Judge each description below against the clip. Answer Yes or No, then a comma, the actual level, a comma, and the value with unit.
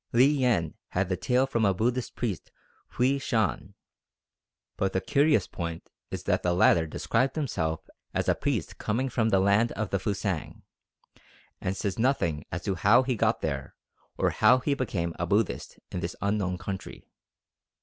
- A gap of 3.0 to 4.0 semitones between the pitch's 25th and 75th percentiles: No, wide, 5.5 semitones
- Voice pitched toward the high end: No, low, 100 Hz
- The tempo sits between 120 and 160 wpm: No, average, 170 wpm